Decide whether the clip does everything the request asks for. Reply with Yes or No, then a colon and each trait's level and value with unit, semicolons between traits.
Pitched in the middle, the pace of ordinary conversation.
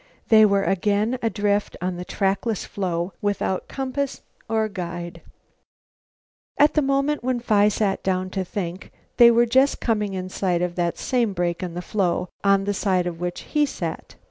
No: high, 200 Hz; average, 170 wpm